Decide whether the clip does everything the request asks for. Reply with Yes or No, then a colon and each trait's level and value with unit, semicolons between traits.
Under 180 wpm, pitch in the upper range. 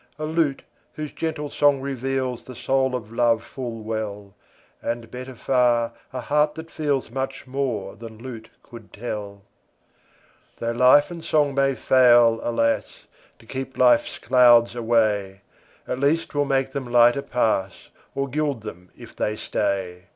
No: average, 150 wpm; low, 125 Hz